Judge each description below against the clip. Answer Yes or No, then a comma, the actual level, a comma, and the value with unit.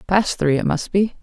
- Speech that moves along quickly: Yes, fast, 245 wpm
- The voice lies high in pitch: No, medium, 180 Hz